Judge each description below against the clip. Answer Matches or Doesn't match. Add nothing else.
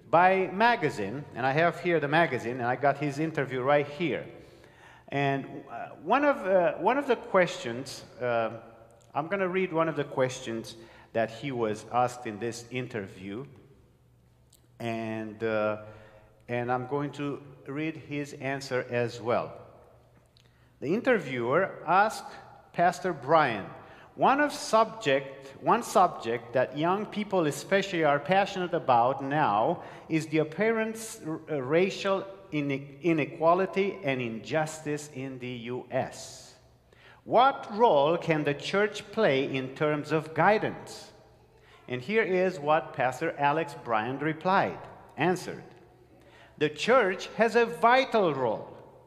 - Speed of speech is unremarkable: Doesn't match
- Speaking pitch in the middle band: Matches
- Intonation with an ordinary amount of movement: Doesn't match